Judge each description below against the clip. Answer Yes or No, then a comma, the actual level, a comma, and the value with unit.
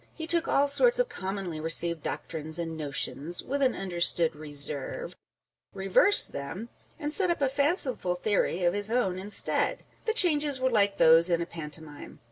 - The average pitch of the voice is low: No, high, 190 Hz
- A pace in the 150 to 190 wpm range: Yes, average, 170 wpm